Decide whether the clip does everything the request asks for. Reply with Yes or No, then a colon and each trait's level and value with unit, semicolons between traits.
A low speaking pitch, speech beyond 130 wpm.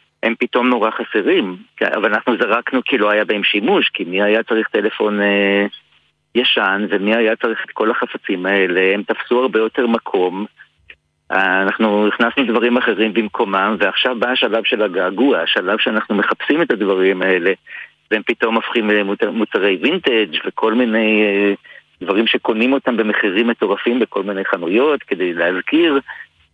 Yes: low, 110 Hz; average, 145 wpm